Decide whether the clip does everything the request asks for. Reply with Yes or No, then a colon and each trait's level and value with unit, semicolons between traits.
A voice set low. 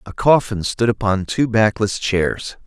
Yes: low, 105 Hz